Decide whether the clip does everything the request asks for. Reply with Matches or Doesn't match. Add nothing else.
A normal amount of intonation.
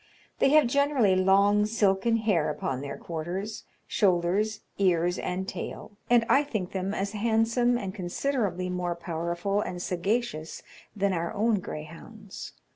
Matches